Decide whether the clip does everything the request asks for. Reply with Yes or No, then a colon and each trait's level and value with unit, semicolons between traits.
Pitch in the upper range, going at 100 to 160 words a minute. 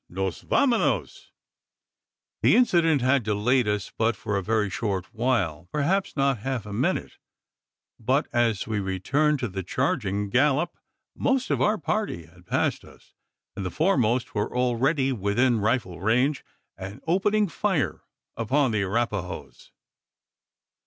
No: low, 120 Hz; slow, 135 wpm